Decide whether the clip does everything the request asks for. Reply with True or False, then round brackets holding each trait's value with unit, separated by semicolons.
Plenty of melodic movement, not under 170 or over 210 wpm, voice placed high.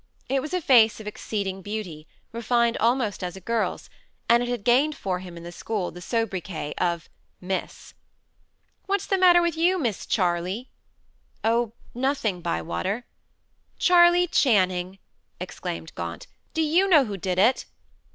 False (6.6 semitones; 150 wpm; 220 Hz)